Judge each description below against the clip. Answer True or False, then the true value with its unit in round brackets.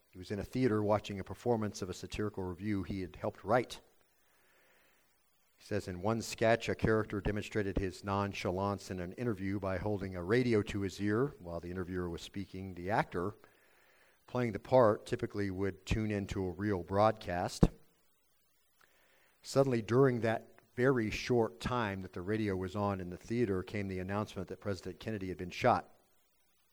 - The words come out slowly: False (170 wpm)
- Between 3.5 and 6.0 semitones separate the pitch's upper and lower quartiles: False (2.8 semitones)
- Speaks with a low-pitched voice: True (100 Hz)